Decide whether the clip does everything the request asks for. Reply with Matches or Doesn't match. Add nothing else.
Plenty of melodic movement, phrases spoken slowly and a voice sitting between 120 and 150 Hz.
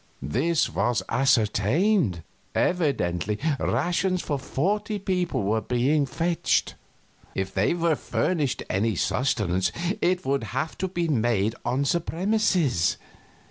Matches